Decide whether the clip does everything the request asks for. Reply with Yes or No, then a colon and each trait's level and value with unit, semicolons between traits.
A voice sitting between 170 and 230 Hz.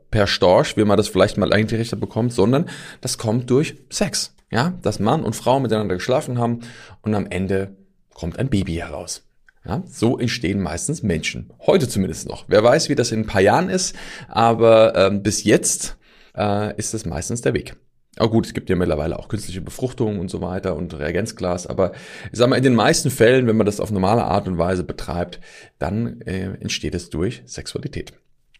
No: low, 105 Hz